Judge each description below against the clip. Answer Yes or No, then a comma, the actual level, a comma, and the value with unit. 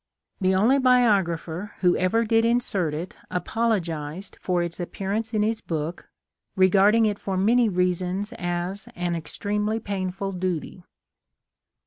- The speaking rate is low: Yes, slow, 125 wpm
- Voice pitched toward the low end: No, high, 190 Hz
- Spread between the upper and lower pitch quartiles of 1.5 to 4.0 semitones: Yes, average, 3.5 semitones